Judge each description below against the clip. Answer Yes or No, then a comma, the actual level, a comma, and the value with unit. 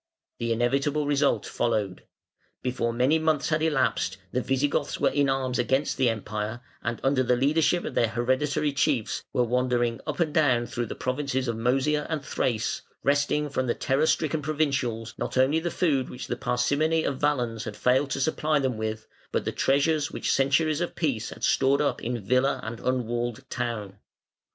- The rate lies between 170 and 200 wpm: Yes, average, 180 wpm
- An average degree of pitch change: Yes, average, 3.5 semitones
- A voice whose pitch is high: No, low, 130 Hz